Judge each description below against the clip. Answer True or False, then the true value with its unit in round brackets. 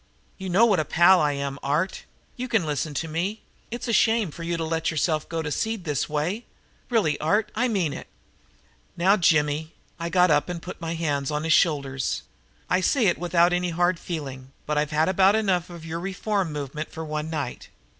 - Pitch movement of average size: True (3.7 semitones)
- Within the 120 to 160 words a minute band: False (205 wpm)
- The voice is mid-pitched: True (165 Hz)